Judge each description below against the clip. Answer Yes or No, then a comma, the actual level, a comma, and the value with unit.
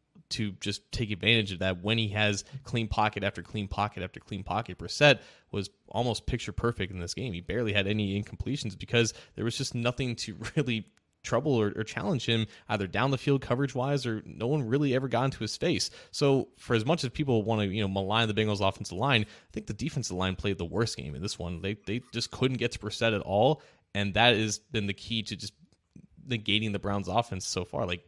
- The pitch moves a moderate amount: Yes, average, 3.1 semitones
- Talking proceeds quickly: Yes, fast, 230 wpm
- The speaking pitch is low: Yes, low, 110 Hz